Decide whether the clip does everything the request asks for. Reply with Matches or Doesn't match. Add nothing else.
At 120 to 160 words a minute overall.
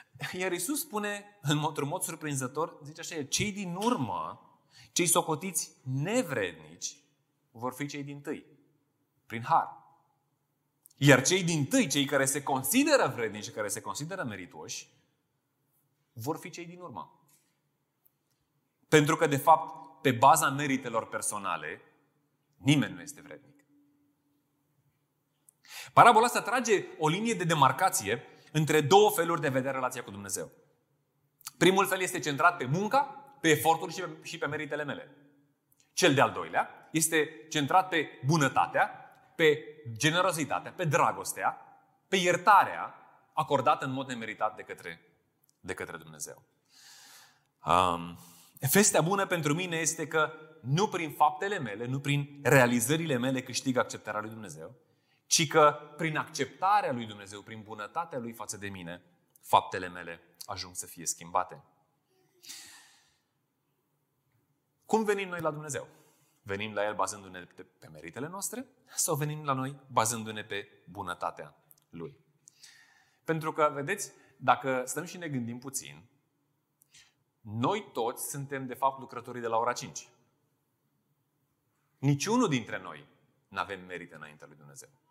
Matches